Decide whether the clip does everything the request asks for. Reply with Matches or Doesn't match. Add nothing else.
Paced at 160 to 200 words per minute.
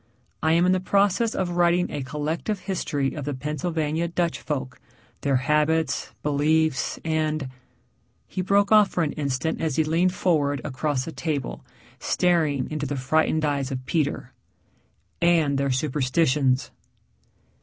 Doesn't match